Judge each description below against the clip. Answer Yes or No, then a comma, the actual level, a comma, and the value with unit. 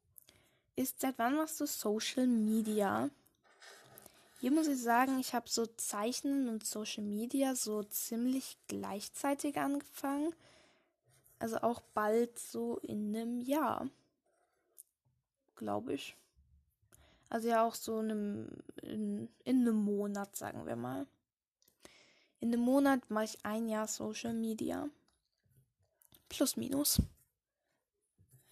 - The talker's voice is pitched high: Yes, high, 230 Hz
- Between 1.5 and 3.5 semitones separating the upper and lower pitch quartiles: No, average, 4.6 semitones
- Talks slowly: Yes, slow, 115 wpm